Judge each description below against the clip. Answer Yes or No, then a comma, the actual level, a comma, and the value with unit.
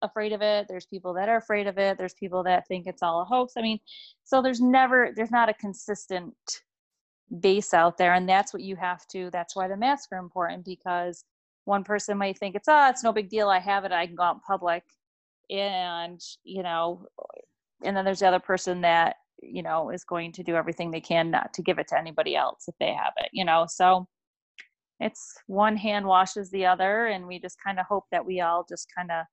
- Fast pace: Yes, fast, 235 wpm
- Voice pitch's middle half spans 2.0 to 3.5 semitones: Yes, average, 2.9 semitones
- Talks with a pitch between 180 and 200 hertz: Yes, high, 190 Hz